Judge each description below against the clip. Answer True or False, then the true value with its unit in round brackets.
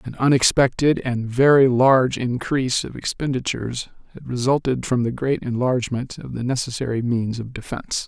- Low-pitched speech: True (125 Hz)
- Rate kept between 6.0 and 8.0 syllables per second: False (5.3 syllables/s)